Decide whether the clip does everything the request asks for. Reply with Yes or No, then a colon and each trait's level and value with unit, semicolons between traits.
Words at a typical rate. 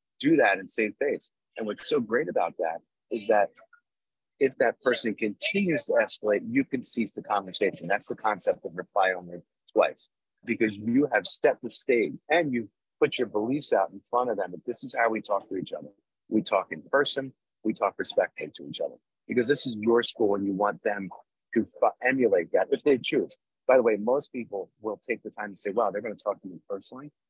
No: fast, 220 wpm